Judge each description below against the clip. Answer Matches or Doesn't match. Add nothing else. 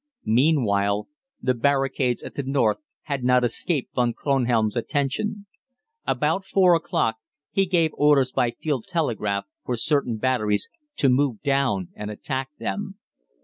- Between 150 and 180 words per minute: Doesn't match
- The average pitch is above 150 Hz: Doesn't match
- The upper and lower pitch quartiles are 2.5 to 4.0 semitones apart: Doesn't match